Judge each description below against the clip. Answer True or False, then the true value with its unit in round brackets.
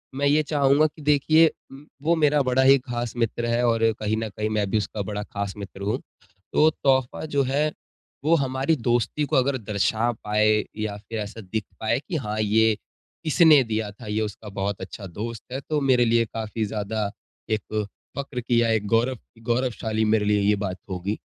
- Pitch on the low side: True (115 Hz)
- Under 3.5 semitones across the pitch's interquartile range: False (4.0 semitones)